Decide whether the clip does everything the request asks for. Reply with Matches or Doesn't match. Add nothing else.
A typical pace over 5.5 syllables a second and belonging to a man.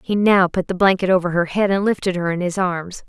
Doesn't match